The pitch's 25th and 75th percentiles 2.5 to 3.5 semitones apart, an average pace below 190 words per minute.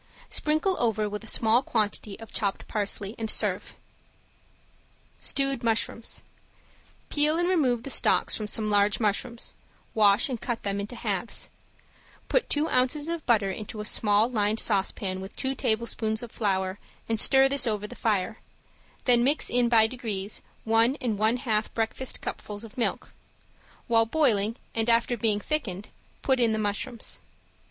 Yes: average, 3.0 semitones; average, 155 wpm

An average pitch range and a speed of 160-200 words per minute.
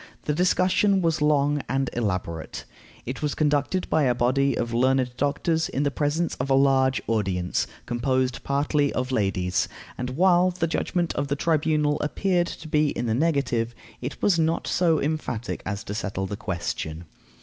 Yes: average, 4.7 semitones; average, 165 wpm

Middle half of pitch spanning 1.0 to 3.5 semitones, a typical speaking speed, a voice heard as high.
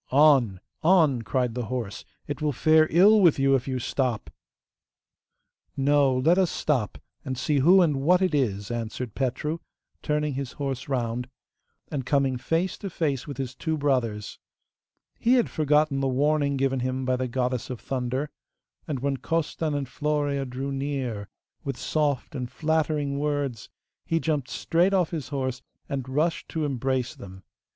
No: average, 3.1 semitones; average, 160 wpm; medium, 140 Hz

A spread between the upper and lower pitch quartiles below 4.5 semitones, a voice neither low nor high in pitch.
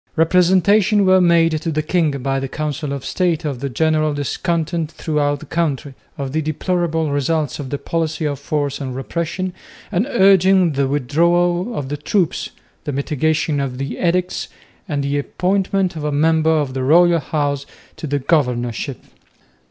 Yes: average, 3.4 semitones; medium, 155 Hz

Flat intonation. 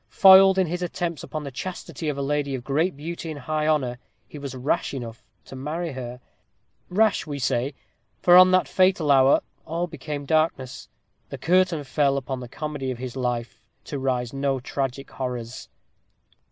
No: average, 4.0 semitones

